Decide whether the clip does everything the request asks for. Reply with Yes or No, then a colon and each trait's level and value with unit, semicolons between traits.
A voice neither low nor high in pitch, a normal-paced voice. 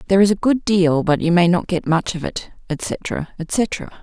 No: medium, 180 Hz; fast, 225 wpm